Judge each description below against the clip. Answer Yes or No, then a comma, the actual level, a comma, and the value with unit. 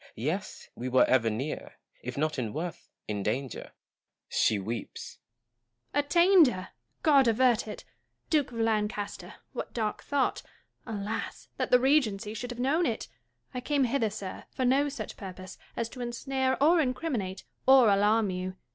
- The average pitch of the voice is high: Yes, high, 225 Hz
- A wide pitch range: Yes, wide, 6.2 semitones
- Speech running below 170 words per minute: Yes, average, 160 wpm